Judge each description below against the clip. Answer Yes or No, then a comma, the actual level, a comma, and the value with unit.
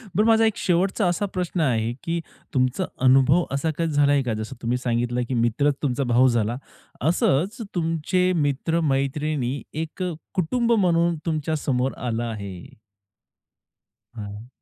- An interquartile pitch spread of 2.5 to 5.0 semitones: No, wide, 5.6 semitones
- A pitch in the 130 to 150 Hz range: Yes, medium, 145 Hz